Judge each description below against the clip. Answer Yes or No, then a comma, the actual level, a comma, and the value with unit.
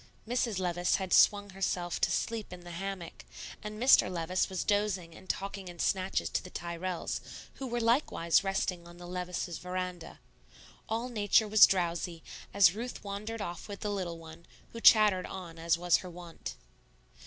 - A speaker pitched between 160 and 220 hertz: Yes, medium, 185 Hz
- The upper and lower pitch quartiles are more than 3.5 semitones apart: No, average, 2.9 semitones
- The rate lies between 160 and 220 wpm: Yes, average, 170 wpm